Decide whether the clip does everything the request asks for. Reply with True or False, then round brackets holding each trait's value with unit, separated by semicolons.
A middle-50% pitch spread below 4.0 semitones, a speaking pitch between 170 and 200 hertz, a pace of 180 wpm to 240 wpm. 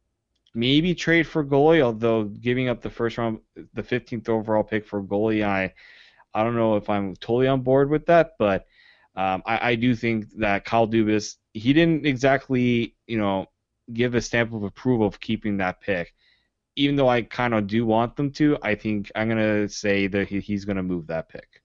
False (3.1 semitones; 115 Hz; 200 wpm)